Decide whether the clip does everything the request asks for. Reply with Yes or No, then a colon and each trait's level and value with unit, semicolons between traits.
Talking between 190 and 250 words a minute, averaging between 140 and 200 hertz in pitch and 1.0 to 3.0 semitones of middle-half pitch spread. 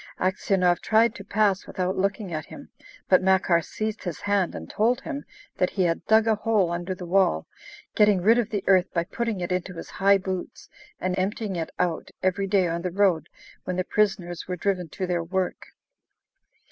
Yes: average, 195 wpm; high, 190 Hz; narrow, 2.4 semitones